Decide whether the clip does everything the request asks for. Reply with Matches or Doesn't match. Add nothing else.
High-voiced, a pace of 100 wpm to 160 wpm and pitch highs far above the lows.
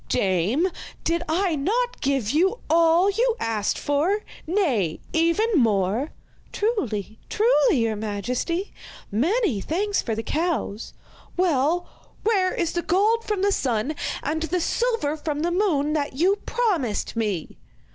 Matches